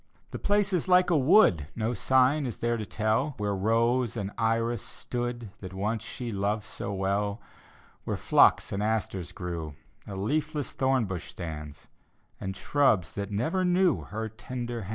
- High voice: No, low, 110 Hz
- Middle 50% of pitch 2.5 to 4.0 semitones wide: No, average, 4.7 semitones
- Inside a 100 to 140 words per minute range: No, average, 160 wpm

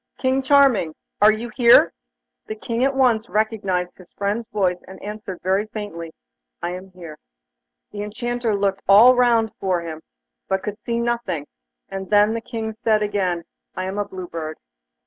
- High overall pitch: Yes, high, 210 Hz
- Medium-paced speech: Yes, average, 165 wpm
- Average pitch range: Yes, average, 3.7 semitones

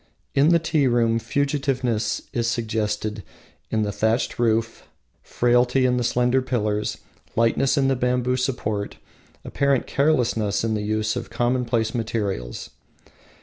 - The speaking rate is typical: No, slow, 130 wpm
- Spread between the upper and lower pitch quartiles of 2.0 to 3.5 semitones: Yes, average, 2.7 semitones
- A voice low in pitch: Yes, low, 120 Hz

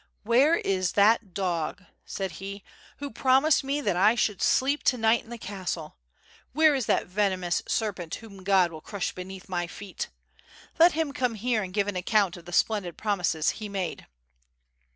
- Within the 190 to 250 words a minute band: No, average, 175 wpm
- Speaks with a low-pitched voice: No, high, 200 Hz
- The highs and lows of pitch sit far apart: No, average, 4.3 semitones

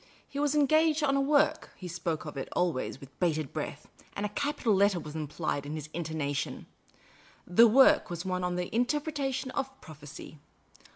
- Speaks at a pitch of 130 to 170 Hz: No, medium, 180 Hz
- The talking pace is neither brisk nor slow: Yes, average, 185 wpm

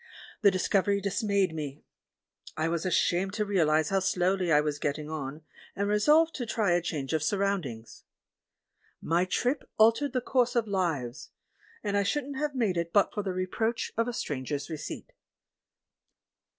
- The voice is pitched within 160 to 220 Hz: Yes, high, 190 Hz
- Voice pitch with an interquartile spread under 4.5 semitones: No, wide, 5.4 semitones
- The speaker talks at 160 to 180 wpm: Yes, average, 165 wpm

